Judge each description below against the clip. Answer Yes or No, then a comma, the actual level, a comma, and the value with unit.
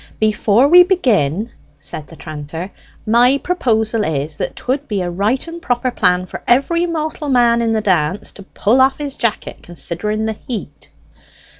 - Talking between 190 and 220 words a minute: No, average, 165 wpm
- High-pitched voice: Yes, high, 220 Hz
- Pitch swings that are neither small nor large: No, wide, 6.4 semitones